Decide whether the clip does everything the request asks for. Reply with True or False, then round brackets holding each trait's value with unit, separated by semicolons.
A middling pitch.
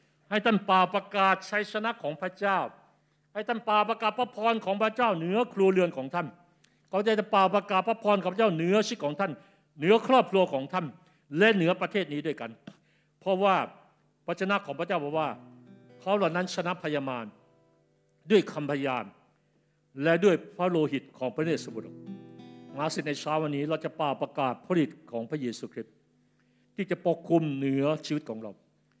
True (170 Hz)